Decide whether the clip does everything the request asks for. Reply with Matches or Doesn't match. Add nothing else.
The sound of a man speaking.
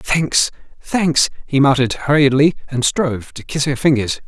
Matches